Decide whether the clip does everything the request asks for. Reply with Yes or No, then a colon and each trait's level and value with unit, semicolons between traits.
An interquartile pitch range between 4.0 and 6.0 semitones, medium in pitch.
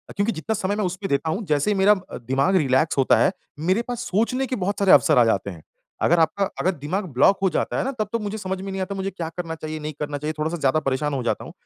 Yes: average, 5.1 semitones; medium, 175 Hz